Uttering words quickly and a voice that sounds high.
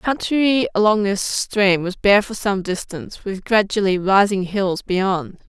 No: average, 160 wpm; high, 200 Hz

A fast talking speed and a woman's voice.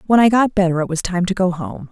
Yes: fast, 315 wpm; female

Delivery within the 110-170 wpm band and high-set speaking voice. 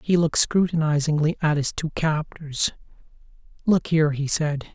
No: average, 140 wpm; medium, 155 Hz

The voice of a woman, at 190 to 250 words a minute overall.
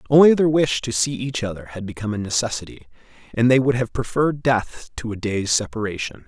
No: male; average, 200 wpm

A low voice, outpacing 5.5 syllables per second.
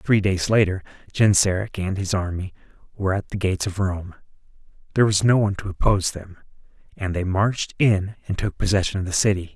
Yes: very low, 95 Hz; 6.0 syllables/s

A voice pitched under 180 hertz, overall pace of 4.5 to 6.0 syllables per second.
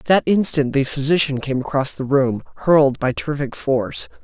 Yes: medium, 140 Hz; 5.3 syllables/s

